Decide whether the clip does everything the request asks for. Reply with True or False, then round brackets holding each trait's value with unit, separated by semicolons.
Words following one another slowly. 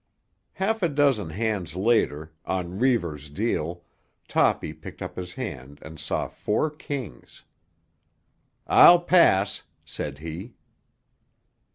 True (105 wpm)